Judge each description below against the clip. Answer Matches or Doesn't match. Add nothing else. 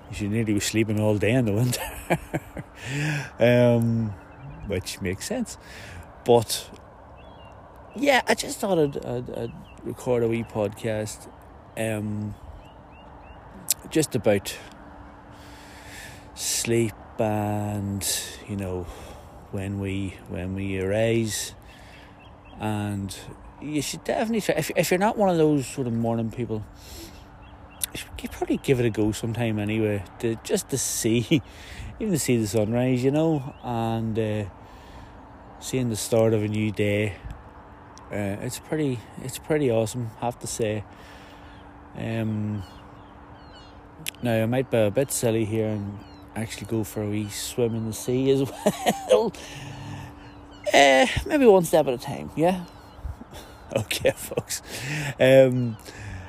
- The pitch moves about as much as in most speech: Matches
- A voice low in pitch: Matches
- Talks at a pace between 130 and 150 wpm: Matches